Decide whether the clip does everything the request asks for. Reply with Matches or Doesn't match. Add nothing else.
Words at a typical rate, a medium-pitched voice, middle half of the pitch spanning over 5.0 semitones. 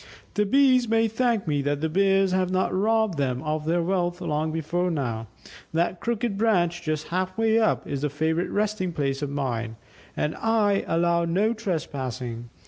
Matches